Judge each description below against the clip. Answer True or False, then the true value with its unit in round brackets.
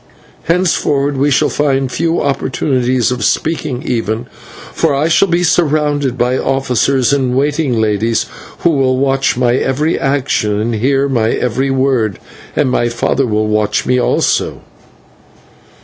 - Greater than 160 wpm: False (140 wpm)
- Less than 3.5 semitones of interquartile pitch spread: True (2.9 semitones)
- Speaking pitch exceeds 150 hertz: False (135 Hz)